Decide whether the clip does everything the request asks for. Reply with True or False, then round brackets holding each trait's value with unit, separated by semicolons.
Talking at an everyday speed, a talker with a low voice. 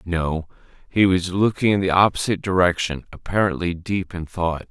True (155 wpm; 90 Hz)